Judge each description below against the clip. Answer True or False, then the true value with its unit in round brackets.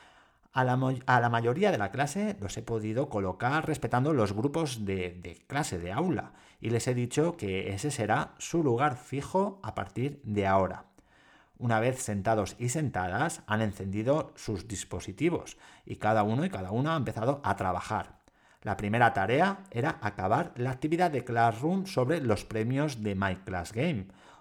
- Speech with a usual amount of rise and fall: False (5.7 semitones)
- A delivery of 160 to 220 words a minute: True (170 wpm)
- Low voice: True (115 Hz)